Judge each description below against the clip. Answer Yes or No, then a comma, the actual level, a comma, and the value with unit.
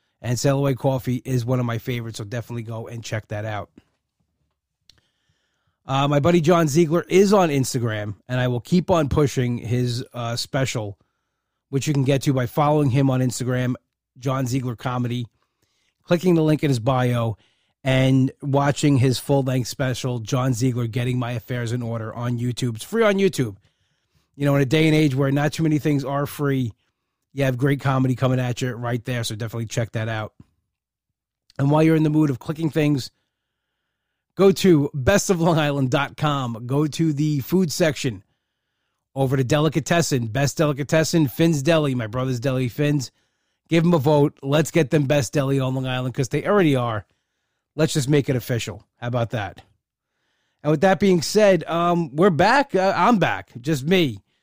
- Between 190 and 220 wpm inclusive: No, average, 180 wpm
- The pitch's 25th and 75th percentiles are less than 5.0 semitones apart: Yes, average, 4.0 semitones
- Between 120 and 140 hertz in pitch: Yes, low, 135 Hz